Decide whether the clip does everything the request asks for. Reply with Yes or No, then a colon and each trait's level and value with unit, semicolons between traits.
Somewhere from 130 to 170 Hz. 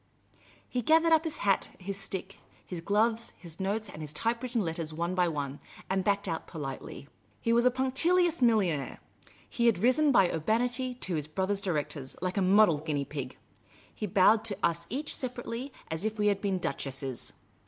No: high, 200 Hz